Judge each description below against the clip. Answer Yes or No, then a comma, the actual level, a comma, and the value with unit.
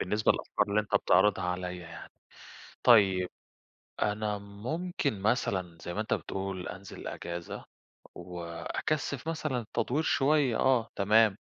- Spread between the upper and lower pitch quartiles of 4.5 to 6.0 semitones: Yes, average, 5.1 semitones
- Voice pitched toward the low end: Yes, low, 105 Hz